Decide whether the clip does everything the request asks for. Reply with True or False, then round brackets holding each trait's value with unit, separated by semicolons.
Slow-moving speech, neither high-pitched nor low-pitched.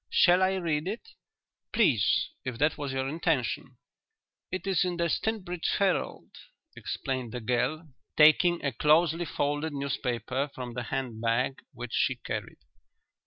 True (130 wpm; 145 Hz)